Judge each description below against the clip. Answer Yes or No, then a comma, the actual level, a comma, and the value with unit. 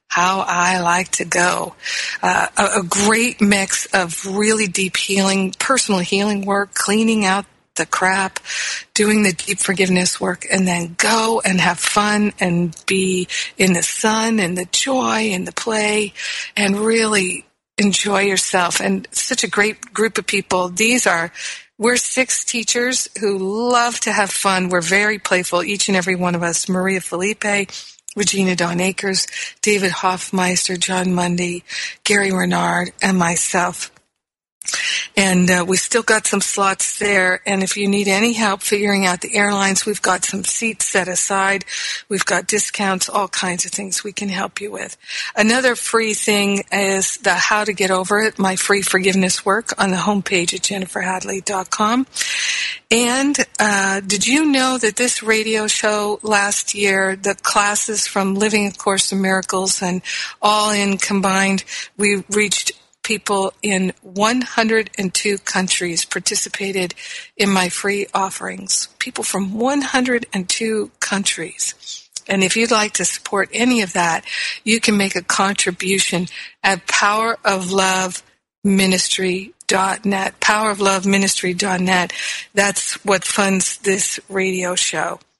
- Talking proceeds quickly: No, average, 140 wpm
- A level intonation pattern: Yes, narrow, 2.1 semitones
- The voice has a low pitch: No, high, 195 Hz